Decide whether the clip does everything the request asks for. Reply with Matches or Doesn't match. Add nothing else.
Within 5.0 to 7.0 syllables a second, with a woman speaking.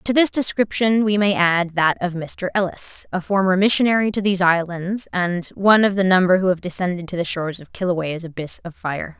Matches